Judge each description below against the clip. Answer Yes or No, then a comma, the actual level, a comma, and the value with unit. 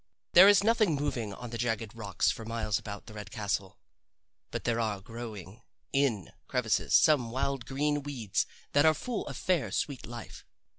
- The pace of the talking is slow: No, average, 170 wpm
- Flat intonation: No, average, 5.1 semitones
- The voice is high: No, low, 120 Hz